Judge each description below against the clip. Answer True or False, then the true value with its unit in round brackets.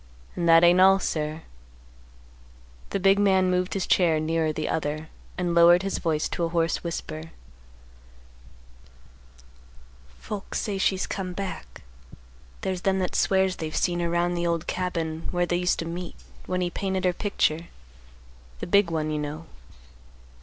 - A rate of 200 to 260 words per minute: False (155 wpm)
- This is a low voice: False (175 Hz)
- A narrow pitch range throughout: True (2.3 semitones)